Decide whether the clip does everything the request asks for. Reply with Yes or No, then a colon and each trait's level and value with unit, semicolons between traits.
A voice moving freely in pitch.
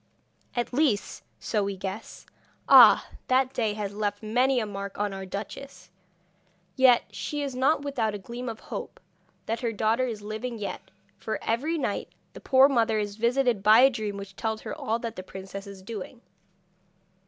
No: average, 3.7 semitones